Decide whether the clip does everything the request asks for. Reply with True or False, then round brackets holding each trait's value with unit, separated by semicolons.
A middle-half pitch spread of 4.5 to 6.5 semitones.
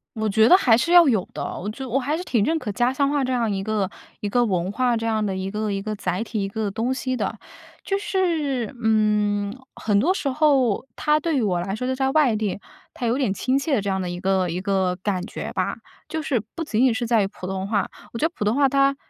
True (5.1 semitones)